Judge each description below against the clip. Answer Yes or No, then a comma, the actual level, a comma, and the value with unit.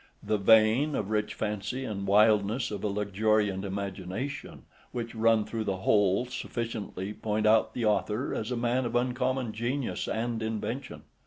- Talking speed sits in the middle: Yes, average, 155 wpm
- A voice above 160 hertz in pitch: No, low, 110 Hz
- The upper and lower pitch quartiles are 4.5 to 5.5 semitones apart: No, narrow, 2.6 semitones